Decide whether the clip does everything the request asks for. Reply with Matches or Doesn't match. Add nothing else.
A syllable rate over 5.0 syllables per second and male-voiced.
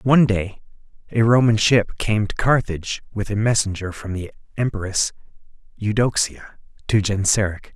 Doesn't match